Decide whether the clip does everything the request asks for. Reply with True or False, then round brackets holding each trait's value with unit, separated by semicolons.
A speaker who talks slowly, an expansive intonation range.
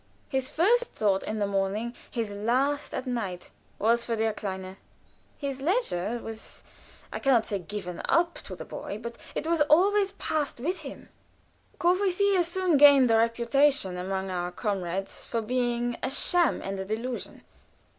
False (160 wpm; 6.5 semitones)